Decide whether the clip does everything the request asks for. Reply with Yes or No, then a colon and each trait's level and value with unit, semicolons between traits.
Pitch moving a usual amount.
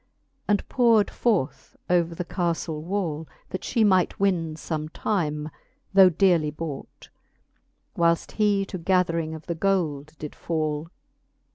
Yes: average, 3.7 semitones